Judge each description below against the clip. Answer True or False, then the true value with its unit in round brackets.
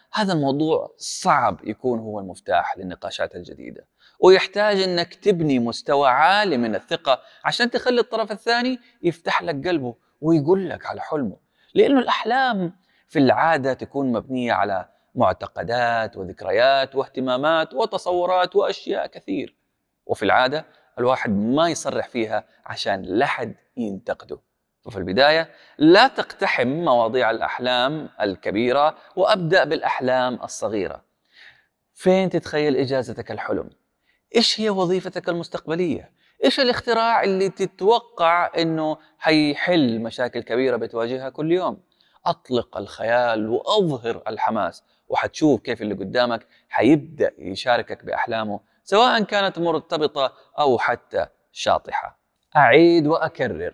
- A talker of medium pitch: True (165 Hz)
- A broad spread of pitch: True (7.9 semitones)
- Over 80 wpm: True (105 wpm)